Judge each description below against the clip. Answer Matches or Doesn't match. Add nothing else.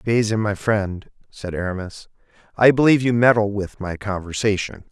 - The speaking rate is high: Doesn't match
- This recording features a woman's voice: Doesn't match